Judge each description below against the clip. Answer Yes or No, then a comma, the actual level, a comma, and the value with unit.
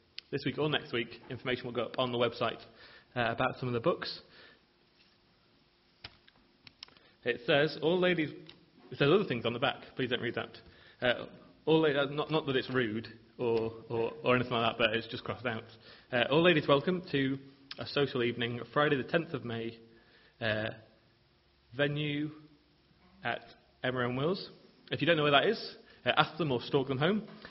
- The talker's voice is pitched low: Yes, low, 125 Hz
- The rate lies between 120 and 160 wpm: No, average, 185 wpm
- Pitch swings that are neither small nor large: Yes, average, 4.1 semitones